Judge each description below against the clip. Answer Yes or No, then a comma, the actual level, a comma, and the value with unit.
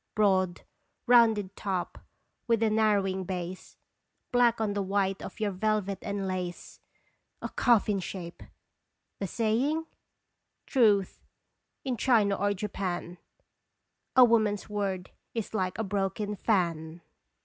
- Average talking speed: No, slow, 115 wpm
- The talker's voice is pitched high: Yes, high, 200 Hz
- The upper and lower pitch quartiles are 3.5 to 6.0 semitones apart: No, average, 2.7 semitones